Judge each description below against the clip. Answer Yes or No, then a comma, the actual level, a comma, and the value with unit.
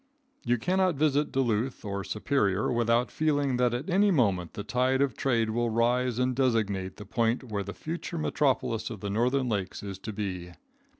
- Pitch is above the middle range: No, low, 120 Hz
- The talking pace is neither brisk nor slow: Yes, average, 180 wpm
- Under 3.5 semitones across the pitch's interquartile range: No, average, 4.4 semitones